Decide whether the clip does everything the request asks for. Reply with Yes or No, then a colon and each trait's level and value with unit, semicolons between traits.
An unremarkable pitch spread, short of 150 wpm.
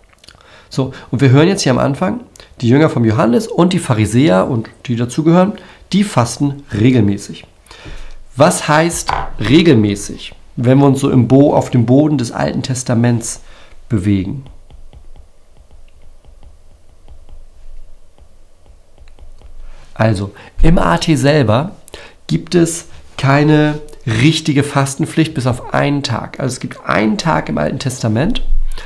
No: wide, 8.2 semitones; slow, 125 wpm